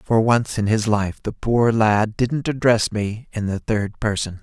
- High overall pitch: No, low, 110 Hz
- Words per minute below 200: No, fast, 205 wpm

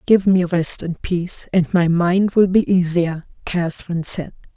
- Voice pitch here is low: No, medium, 175 Hz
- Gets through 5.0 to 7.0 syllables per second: No, 4.5 syllables/s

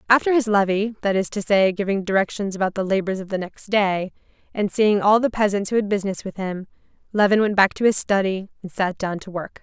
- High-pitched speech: Yes, high, 200 Hz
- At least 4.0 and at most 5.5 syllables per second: No, 5.9 syllables/s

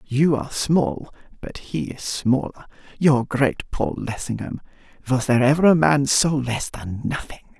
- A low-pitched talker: Yes, low, 130 Hz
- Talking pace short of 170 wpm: Yes, average, 140 wpm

